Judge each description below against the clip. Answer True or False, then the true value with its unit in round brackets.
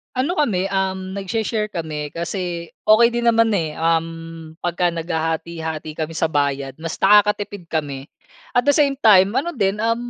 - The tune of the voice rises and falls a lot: False (4.6 semitones)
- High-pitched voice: False (175 Hz)